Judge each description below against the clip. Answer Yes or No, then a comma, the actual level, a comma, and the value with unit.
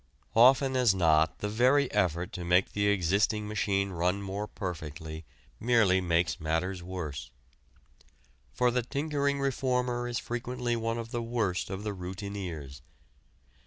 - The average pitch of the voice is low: Yes, low, 100 Hz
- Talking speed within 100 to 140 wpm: Yes, slow, 135 wpm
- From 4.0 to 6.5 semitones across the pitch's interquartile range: Yes, average, 5.3 semitones